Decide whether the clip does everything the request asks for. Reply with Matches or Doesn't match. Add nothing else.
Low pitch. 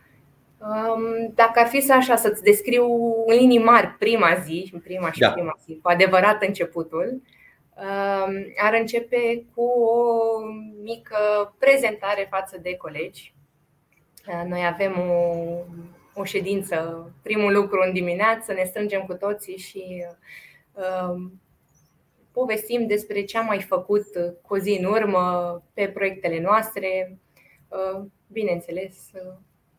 Doesn't match